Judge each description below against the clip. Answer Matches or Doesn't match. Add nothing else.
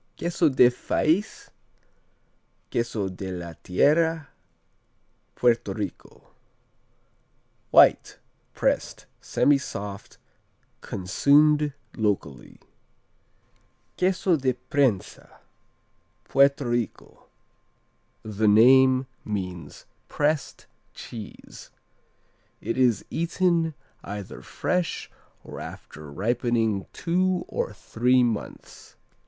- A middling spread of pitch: Doesn't match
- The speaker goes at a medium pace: Doesn't match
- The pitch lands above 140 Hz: Doesn't match